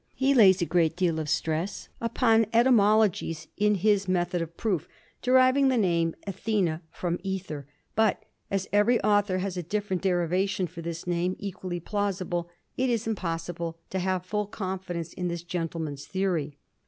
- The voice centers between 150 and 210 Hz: Yes, medium, 185 Hz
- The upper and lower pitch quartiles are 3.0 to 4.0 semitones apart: Yes, average, 3.4 semitones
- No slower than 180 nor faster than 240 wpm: No, average, 155 wpm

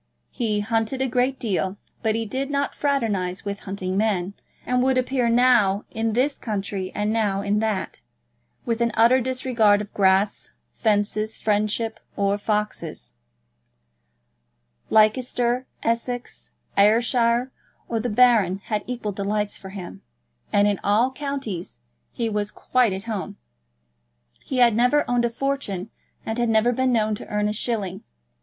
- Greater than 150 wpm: No, average, 145 wpm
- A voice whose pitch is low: No, high, 220 Hz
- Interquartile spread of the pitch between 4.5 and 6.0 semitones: No, average, 3.2 semitones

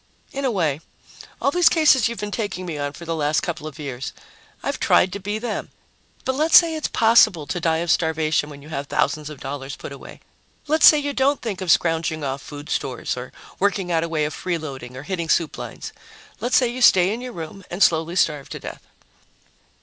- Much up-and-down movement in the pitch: Yes, wide, 6.7 semitones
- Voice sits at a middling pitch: Yes, medium, 170 Hz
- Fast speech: Yes, fast, 220 wpm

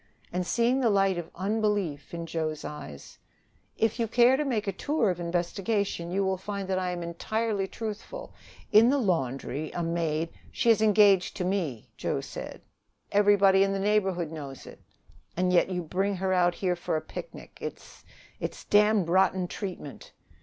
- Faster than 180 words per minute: No, average, 175 wpm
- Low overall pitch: No, high, 190 Hz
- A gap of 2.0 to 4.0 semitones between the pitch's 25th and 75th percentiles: Yes, average, 3.4 semitones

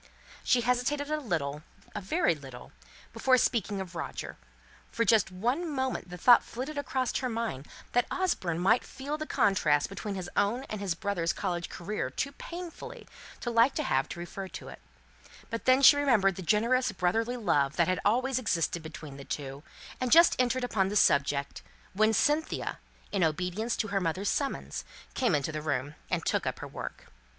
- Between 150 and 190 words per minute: Yes, average, 180 wpm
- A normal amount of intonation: No, wide, 6.9 semitones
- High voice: Yes, high, 210 Hz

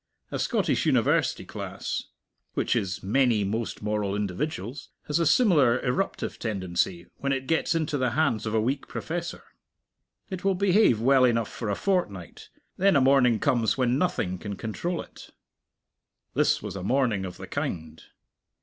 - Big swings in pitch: Yes, wide, 6.6 semitones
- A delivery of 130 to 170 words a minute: Yes, average, 160 wpm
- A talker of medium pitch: No, low, 120 Hz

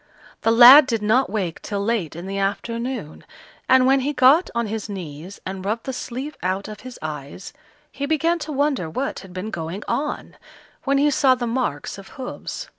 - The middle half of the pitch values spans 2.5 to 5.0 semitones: No, wide, 5.6 semitones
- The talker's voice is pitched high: Yes, high, 230 Hz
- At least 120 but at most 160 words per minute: No, average, 190 wpm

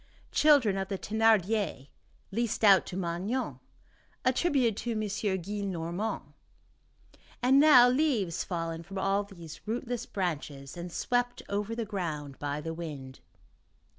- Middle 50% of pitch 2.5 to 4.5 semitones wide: No, average, 5.3 semitones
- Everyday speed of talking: No, slow, 125 wpm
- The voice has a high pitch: Yes, high, 200 Hz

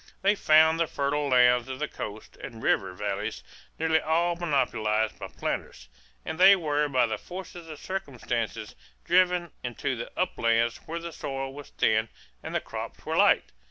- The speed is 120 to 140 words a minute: No, average, 165 wpm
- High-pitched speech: No, medium, 145 Hz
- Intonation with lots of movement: Yes, wide, 5.9 semitones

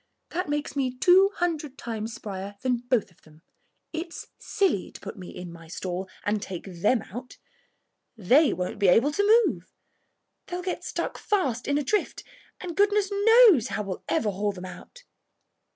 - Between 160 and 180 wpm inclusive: Yes, average, 170 wpm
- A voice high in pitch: Yes, very high, 250 Hz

